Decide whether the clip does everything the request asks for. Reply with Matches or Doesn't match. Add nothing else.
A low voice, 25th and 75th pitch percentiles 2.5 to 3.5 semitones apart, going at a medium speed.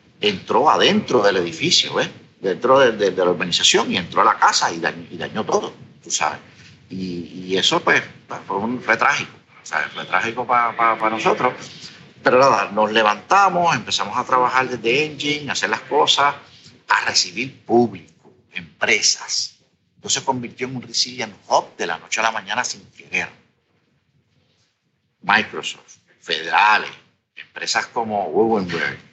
Matches